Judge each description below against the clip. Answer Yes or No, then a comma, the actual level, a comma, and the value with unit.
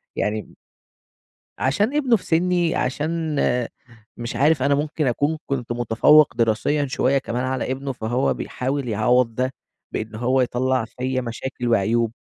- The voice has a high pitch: No, low, 130 Hz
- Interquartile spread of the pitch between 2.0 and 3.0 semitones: No, average, 3.5 semitones